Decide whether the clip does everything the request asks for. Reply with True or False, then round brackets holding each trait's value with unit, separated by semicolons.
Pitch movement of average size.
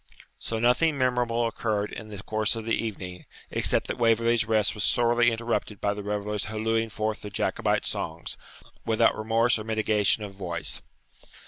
False (1.8 semitones)